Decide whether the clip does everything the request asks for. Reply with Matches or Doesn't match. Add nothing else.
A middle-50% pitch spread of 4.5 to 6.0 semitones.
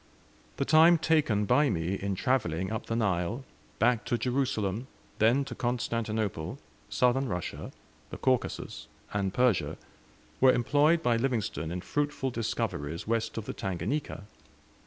Matches